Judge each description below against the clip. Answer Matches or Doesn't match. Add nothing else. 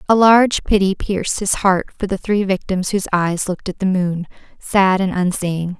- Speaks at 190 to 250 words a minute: Matches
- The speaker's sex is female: Matches